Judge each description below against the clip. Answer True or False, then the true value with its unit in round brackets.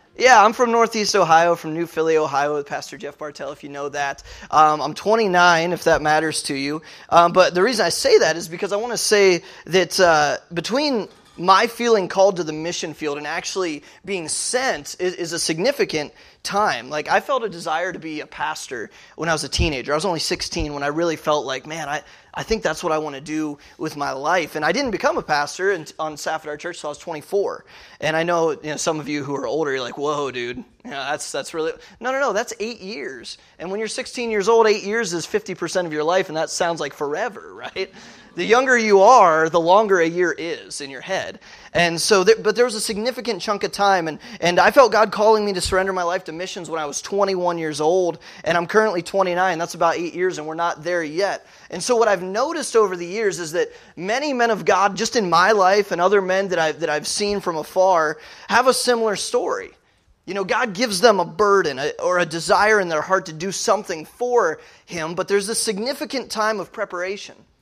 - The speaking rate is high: True (235 wpm)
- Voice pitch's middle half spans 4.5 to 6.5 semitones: True (5.2 semitones)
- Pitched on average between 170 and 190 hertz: True (185 Hz)